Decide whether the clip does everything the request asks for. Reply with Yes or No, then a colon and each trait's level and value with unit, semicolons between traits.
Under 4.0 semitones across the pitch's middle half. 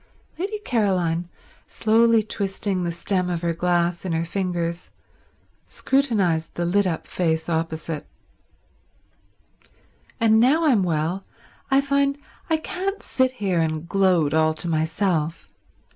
No: wide, 5.4 semitones